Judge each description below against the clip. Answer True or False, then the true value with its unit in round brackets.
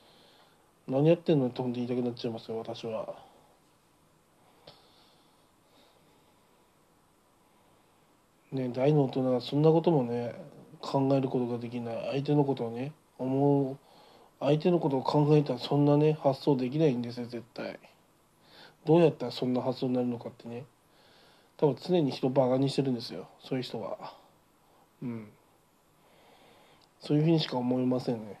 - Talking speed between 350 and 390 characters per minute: False (295 characters per minute)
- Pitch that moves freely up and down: False (3.2 semitones)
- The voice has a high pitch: False (130 Hz)